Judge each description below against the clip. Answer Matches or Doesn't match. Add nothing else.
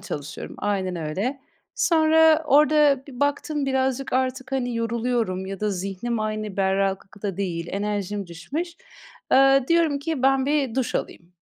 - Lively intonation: Matches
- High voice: Matches